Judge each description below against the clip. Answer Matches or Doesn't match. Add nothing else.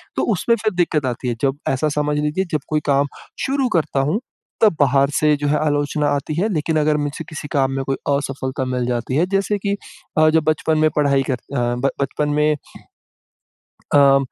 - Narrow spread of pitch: Matches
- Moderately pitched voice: Matches